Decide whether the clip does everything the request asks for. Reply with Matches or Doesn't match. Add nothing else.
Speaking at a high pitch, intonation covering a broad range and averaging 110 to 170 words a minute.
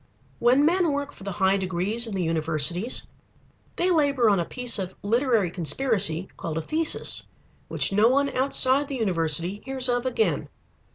Matches